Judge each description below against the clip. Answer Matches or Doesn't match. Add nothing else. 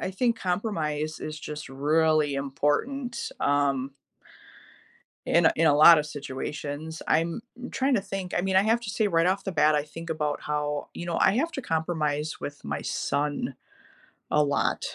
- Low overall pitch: Doesn't match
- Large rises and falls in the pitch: Doesn't match